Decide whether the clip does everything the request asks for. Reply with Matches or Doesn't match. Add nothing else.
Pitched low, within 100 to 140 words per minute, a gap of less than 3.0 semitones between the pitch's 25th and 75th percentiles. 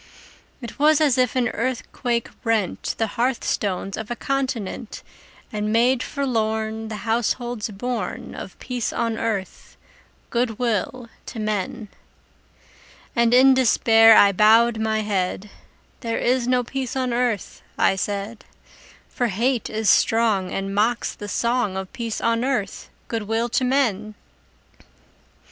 Doesn't match